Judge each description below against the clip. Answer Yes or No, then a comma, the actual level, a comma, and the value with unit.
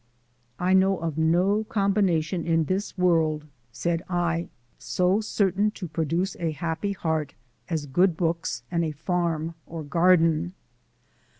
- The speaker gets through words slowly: Yes, slow, 130 wpm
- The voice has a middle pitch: Yes, medium, 170 Hz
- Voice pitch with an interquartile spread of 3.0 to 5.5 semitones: No, narrow, 2.6 semitones